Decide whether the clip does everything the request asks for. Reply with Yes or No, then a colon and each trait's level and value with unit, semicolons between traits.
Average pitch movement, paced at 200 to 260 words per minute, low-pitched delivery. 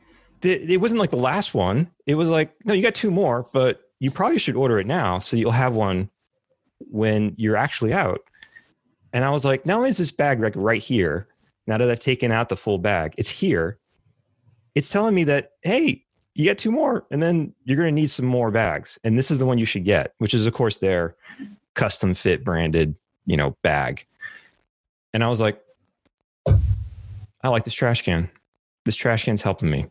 No: wide, 6.7 semitones; fast, 205 wpm; low, 120 Hz